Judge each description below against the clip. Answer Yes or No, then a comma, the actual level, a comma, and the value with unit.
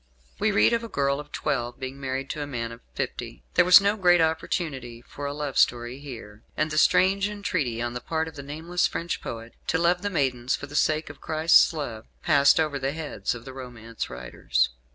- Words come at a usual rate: No, fast, 215 wpm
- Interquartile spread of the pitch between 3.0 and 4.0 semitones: No, average, 5.0 semitones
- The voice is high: No, medium, 140 Hz